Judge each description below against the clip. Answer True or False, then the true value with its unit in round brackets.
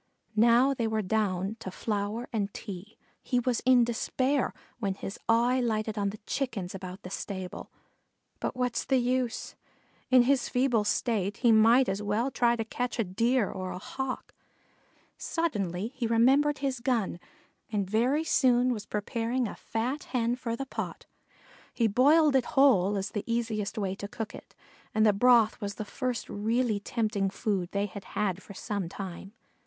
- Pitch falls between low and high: False (225 Hz)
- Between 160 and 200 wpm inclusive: True (170 wpm)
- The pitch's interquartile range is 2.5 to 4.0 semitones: True (3.7 semitones)